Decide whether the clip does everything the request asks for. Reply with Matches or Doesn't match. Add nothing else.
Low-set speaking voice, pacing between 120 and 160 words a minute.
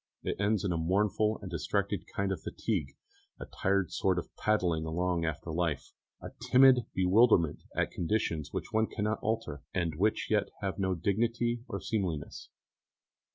Matches